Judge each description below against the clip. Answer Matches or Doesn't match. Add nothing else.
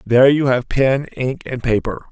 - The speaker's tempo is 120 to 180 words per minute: Doesn't match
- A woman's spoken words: Doesn't match